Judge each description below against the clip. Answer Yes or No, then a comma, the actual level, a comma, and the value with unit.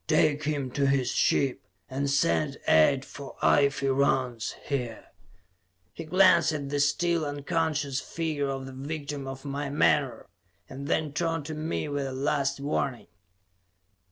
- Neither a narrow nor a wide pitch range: No, narrow, 1.9 semitones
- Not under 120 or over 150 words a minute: Yes, average, 145 wpm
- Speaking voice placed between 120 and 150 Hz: Yes, medium, 140 Hz